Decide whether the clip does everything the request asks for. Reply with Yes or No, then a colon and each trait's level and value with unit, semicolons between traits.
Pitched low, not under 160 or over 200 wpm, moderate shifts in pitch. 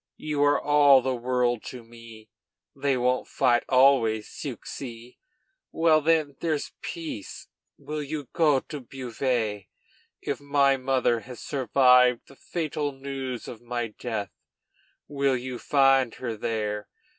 No: low, 130 Hz; slow, 135 wpm; average, 3.1 semitones